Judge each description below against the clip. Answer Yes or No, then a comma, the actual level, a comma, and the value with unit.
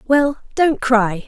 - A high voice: Yes, very high, 255 Hz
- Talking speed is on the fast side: No, average, 140 wpm